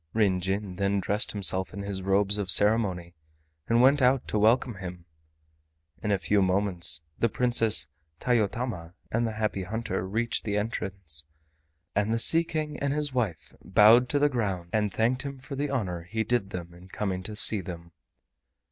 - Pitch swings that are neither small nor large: Yes, average, 3.9 semitones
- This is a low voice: Yes, low, 105 Hz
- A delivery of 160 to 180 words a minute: Yes, average, 175 wpm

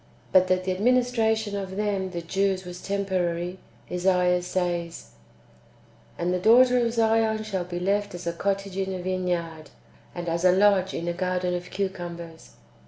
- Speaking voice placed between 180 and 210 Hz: Yes, medium, 185 Hz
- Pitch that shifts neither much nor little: No, narrow, 2.2 semitones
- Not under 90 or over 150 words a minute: No, average, 170 wpm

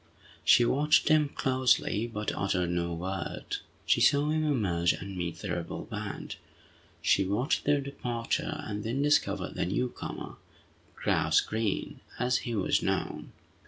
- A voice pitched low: Yes, low, 110 Hz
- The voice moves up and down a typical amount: No, wide, 6.1 semitones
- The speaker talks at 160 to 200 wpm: No, average, 140 wpm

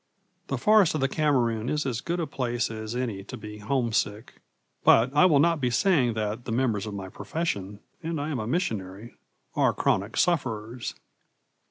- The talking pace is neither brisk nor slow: Yes, average, 180 wpm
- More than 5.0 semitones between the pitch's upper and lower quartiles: Yes, wide, 5.6 semitones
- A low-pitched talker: Yes, low, 120 Hz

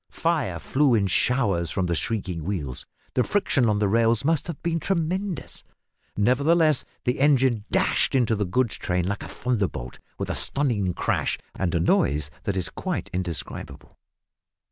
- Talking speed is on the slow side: No, average, 160 wpm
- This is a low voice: Yes, low, 115 Hz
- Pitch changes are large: Yes, wide, 7.3 semitones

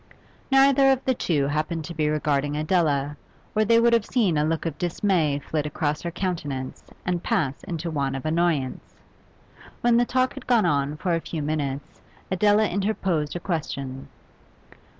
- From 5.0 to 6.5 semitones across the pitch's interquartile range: Yes, average, 5.3 semitones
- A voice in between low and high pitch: Yes, medium, 165 Hz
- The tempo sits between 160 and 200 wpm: Yes, average, 170 wpm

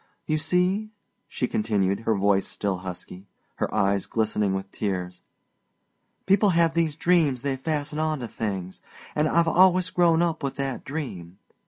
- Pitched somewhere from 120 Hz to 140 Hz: Yes, low, 135 Hz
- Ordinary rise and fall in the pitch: No, wide, 8.8 semitones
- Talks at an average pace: Yes, average, 150 wpm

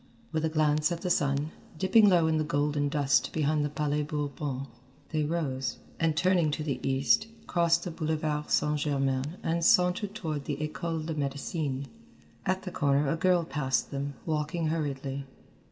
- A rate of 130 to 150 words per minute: No, average, 170 wpm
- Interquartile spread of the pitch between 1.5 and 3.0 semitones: Yes, narrow, 2.5 semitones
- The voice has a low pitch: No, medium, 150 Hz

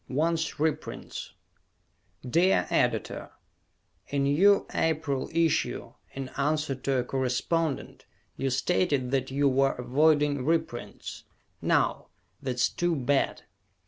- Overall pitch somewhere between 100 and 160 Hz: Yes, medium, 140 Hz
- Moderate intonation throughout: Yes, average, 3.3 semitones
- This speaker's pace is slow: Yes, slow, 110 wpm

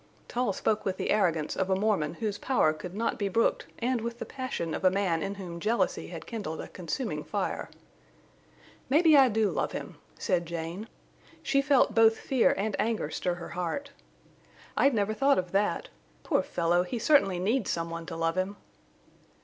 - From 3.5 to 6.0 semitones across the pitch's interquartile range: Yes, average, 5.1 semitones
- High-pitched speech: Yes, high, 200 Hz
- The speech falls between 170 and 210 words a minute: Yes, average, 185 wpm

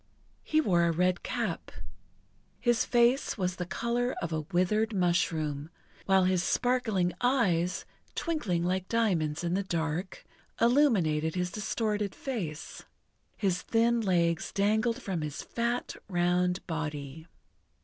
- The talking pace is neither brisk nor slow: No, slow, 125 wpm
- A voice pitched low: No, medium, 185 Hz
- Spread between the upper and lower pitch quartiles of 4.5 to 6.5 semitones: Yes, average, 5.2 semitones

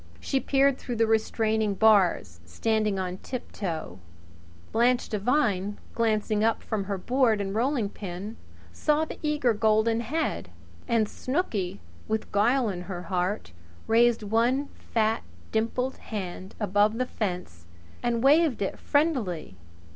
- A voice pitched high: Yes, high, 220 Hz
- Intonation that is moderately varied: Yes, average, 3.6 semitones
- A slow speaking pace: Yes, slow, 130 wpm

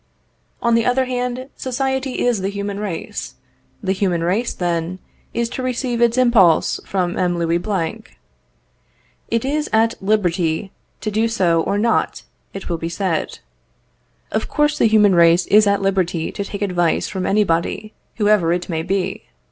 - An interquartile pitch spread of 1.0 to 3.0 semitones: No, average, 4.8 semitones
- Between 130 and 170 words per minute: Yes, average, 160 wpm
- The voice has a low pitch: No, high, 200 Hz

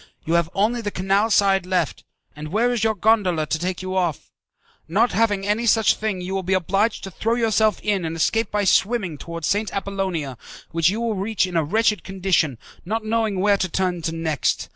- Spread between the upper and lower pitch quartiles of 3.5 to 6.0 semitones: Yes, average, 3.8 semitones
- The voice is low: No, high, 195 Hz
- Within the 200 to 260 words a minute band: Yes, fast, 205 wpm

